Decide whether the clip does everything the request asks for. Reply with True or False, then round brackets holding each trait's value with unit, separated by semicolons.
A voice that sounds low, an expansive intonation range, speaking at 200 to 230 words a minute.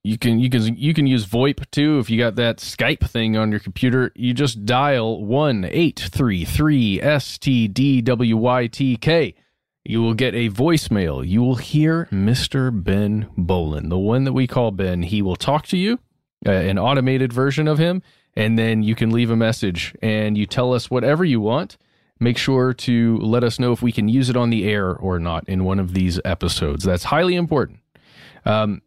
False (120 Hz; 4.0 semitones; 205 wpm)